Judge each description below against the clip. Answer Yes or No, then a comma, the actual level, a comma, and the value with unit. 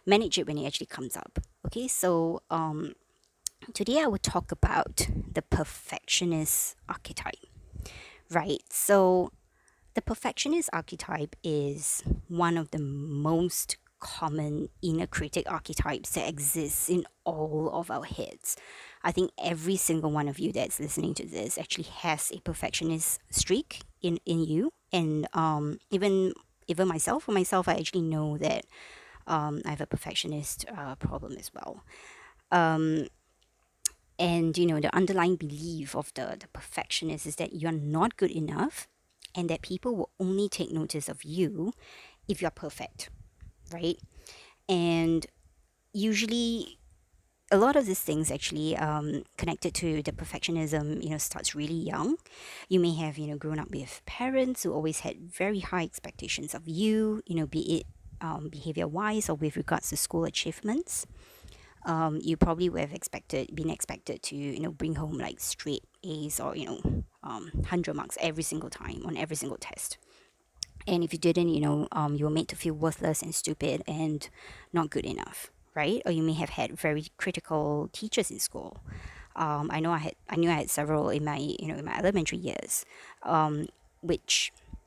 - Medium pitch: Yes, medium, 165 Hz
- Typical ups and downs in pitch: Yes, average, 3.0 semitones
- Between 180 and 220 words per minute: No, average, 165 wpm